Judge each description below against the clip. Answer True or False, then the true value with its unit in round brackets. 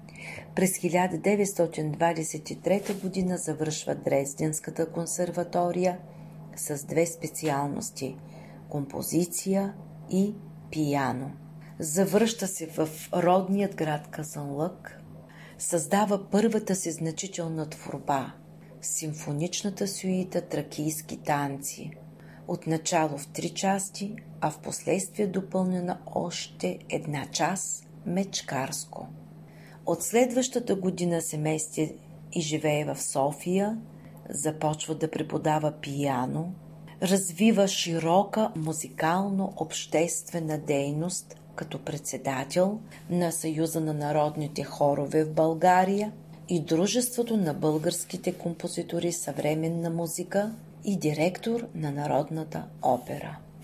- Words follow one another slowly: True (85 wpm)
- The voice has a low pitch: False (165 Hz)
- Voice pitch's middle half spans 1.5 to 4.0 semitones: True (3.0 semitones)